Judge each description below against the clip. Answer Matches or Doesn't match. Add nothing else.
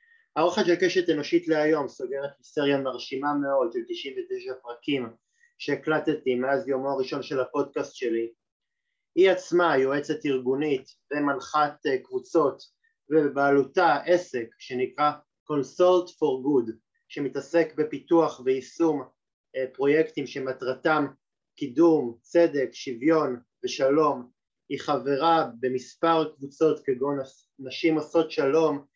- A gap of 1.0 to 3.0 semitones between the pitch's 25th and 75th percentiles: Doesn't match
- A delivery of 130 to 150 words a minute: Doesn't match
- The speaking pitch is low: Doesn't match